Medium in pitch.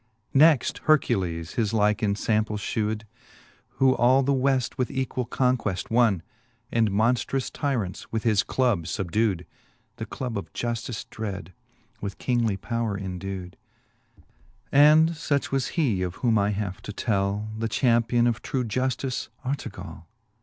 No: low, 115 Hz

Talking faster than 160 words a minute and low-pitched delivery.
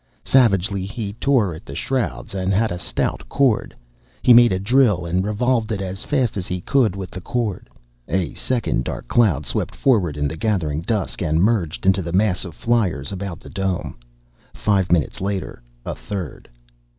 Yes: average, 180 wpm; low, 100 Hz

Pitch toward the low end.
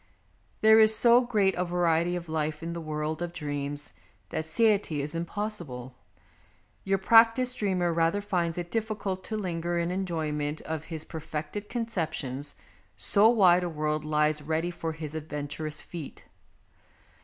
No: medium, 170 Hz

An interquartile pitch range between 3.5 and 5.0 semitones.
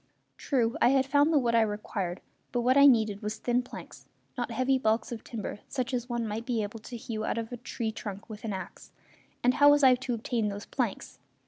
No: average, 2.7 semitones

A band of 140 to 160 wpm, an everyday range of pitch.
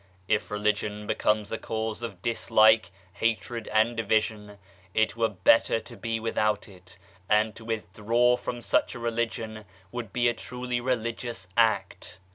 No: average, 145 wpm; narrow, 1.8 semitones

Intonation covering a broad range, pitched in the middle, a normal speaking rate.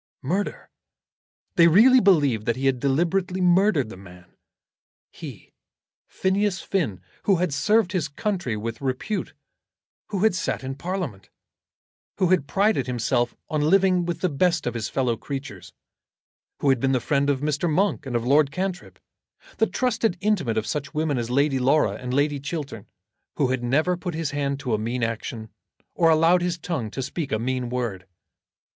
Yes: wide, 6.2 semitones; medium, 145 Hz; average, 170 wpm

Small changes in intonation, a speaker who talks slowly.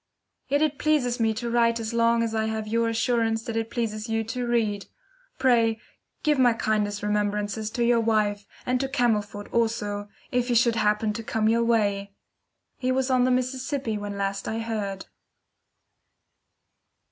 No: narrow, 2.3 semitones; average, 170 wpm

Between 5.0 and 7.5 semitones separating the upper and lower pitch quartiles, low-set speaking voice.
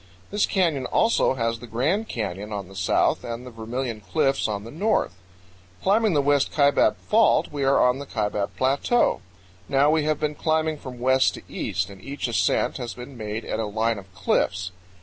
Yes: average, 5.3 semitones; low, 130 Hz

